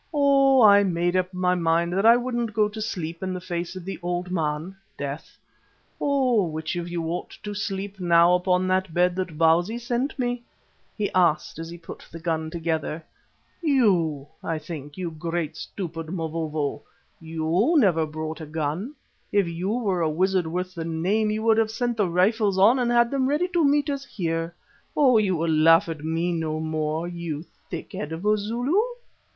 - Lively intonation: No, average, 4.7 semitones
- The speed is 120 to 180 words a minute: No, average, 190 wpm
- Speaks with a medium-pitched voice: Yes, medium, 180 Hz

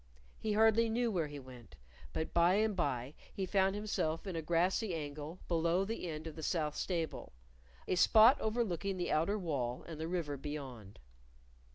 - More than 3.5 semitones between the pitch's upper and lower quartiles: Yes, average, 4.8 semitones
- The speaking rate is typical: Yes, average, 175 wpm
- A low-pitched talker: No, medium, 170 Hz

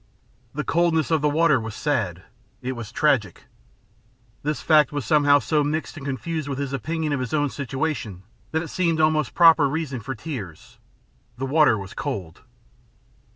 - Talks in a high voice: No, medium, 145 Hz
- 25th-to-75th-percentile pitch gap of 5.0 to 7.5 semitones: No, average, 3.6 semitones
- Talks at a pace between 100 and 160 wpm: No, average, 170 wpm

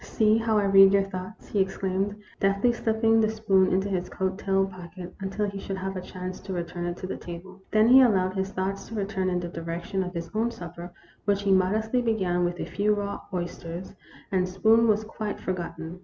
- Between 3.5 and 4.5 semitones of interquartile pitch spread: No, narrow, 2.5 semitones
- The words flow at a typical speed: No, fast, 230 wpm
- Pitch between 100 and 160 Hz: No, high, 195 Hz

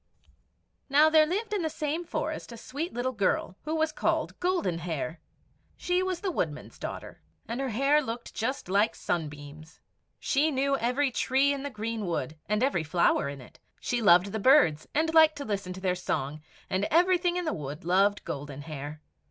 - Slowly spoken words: No, average, 185 wpm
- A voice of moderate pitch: No, high, 235 Hz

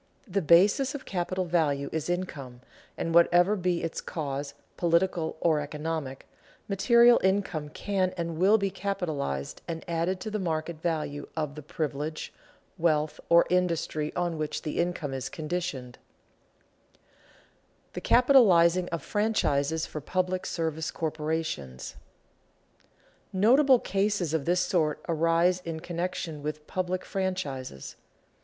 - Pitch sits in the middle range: Yes, medium, 170 Hz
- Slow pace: Yes, slow, 125 wpm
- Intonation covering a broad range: No, average, 3.3 semitones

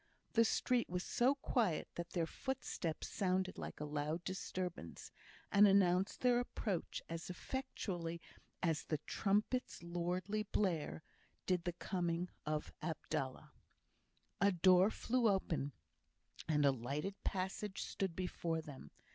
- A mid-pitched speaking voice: Yes, medium, 180 Hz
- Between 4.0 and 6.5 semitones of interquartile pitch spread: No, average, 3.5 semitones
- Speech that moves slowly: Yes, slow, 125 wpm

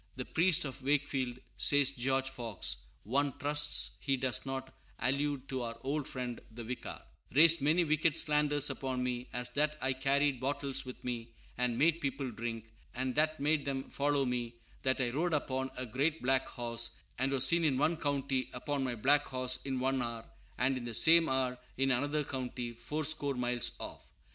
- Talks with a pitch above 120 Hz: Yes, low, 135 Hz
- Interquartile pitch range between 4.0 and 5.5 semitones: No, narrow, 2.6 semitones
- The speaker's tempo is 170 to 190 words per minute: Yes, average, 180 wpm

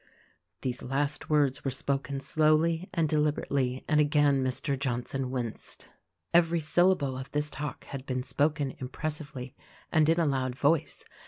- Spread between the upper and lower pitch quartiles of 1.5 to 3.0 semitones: Yes, average, 2.7 semitones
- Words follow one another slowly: No, average, 145 wpm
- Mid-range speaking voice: Yes, medium, 145 Hz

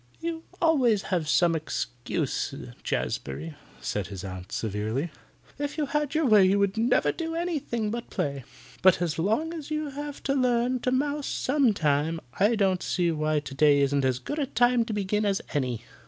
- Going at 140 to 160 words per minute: No, average, 180 wpm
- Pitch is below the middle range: No, high, 200 Hz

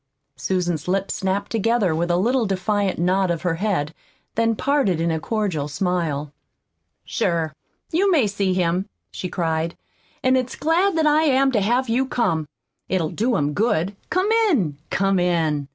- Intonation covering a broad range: Yes, wide, 6.0 semitones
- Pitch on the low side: No, high, 190 Hz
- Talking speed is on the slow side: No, average, 165 wpm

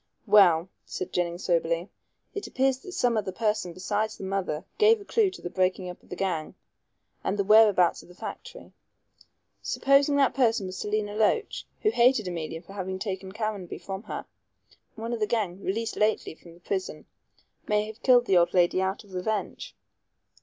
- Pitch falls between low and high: No, high, 200 Hz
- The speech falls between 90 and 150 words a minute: No, average, 180 wpm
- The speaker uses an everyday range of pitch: Yes, average, 3.8 semitones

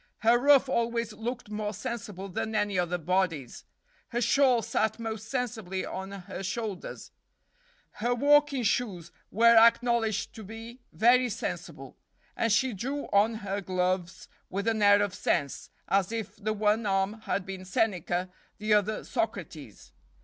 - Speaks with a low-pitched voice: No, high, 215 Hz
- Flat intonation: No, average, 3.3 semitones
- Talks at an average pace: Yes, average, 145 wpm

